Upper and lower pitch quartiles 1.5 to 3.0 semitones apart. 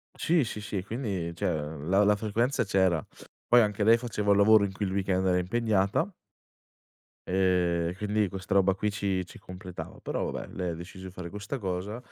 Yes: narrow, 2.5 semitones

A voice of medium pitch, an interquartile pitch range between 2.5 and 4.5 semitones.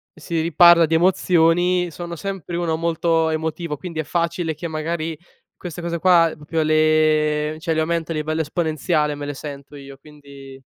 No: medium, 160 Hz; narrow, 1.8 semitones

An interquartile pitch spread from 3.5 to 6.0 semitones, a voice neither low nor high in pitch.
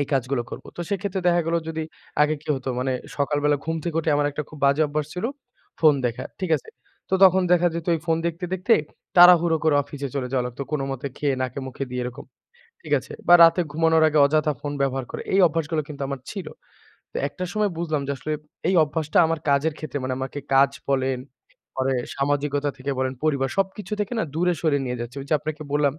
No: average, 3.1 semitones; medium, 150 Hz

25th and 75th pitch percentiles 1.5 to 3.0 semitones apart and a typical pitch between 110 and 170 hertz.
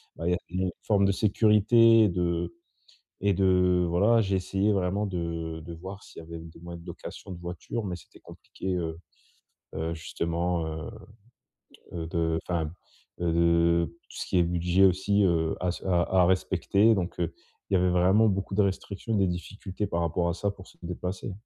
No: narrow, 2.5 semitones; very low, 90 Hz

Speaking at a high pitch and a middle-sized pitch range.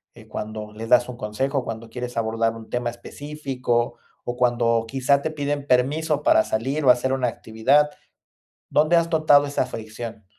No: low, 125 Hz; average, 3.9 semitones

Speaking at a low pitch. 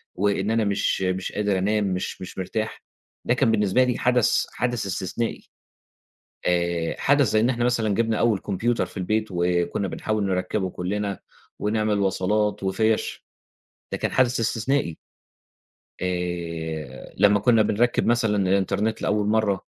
Yes: low, 105 Hz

